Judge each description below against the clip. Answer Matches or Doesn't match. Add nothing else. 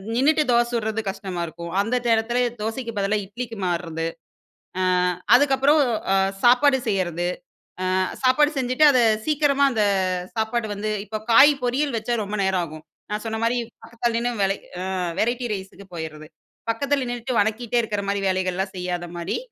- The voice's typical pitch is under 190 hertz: Doesn't match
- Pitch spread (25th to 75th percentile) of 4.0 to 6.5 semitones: Matches